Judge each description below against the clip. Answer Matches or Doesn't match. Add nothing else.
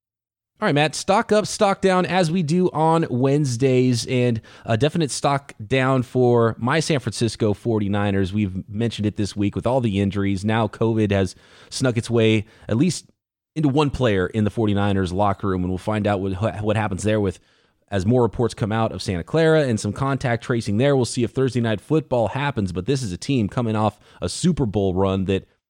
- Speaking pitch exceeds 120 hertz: Doesn't match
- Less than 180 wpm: Doesn't match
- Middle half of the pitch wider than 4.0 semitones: Matches